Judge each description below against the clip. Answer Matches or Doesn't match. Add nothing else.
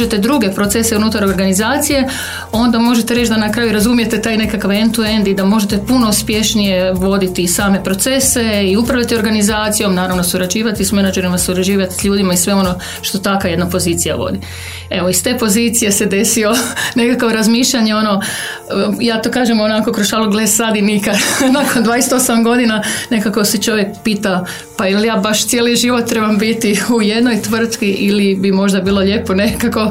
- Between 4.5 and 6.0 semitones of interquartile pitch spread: Doesn't match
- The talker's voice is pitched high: Matches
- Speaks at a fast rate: Matches